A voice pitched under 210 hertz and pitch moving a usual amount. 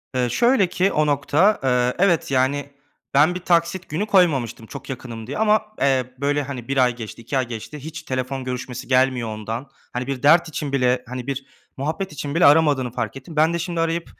Yes: medium, 140 Hz; average, 4.4 semitones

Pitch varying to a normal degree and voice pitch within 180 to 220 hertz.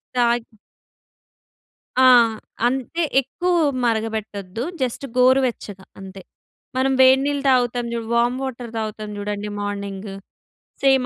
No: average, 3.6 semitones; high, 235 Hz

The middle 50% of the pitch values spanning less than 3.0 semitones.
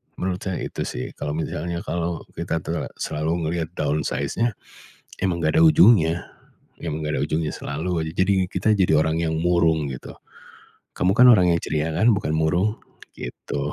Yes: narrow, 2.4 semitones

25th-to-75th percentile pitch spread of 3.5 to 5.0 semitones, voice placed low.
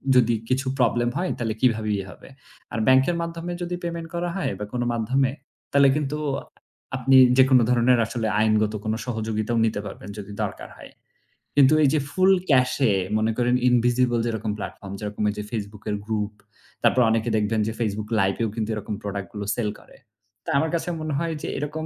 Yes: average, 3.9 semitones; low, 120 Hz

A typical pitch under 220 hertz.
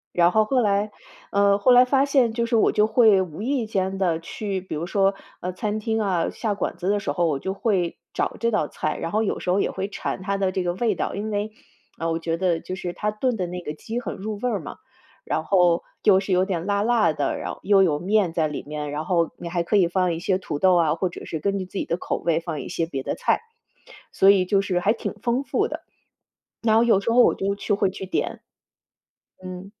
Yes: high, 190 Hz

